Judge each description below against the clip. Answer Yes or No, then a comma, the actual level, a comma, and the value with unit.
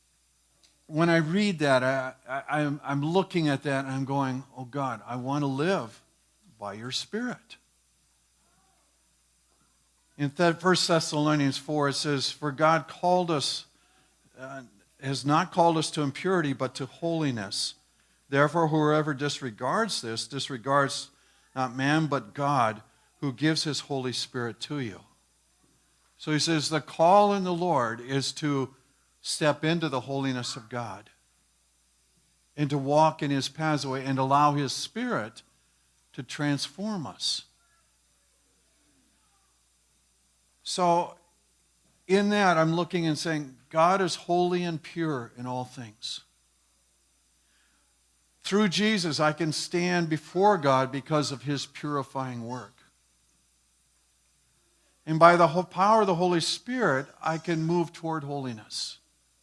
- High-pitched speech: No, medium, 140 Hz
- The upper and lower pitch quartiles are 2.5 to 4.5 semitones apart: No, average, 5.1 semitones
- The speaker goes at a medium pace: No, slow, 130 wpm